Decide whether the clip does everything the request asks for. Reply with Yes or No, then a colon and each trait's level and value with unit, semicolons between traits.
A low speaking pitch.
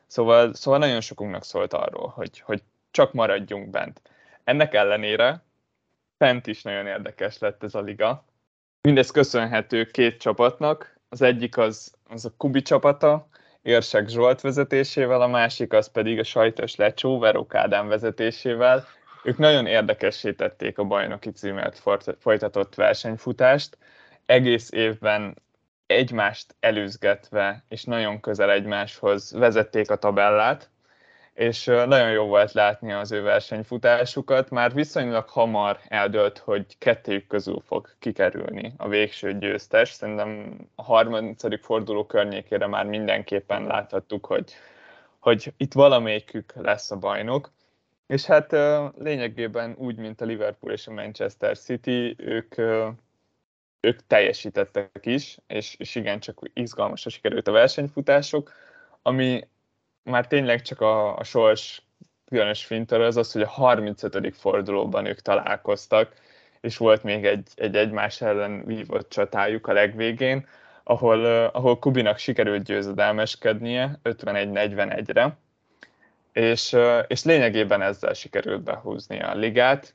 Yes: low, 115 Hz